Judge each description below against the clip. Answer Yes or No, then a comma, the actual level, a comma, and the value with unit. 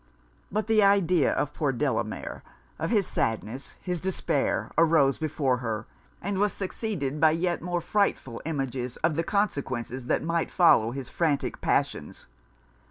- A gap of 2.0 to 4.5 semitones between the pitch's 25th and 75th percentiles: No, wide, 5.6 semitones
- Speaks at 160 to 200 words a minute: No, average, 145 wpm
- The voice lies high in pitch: No, medium, 160 Hz